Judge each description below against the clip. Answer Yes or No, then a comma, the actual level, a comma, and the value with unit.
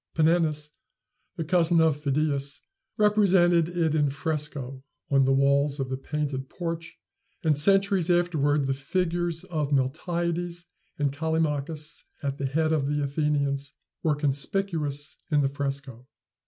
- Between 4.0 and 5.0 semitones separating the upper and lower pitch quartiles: No, average, 3.2 semitones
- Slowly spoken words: Yes, slow, 130 wpm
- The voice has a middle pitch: Yes, medium, 150 Hz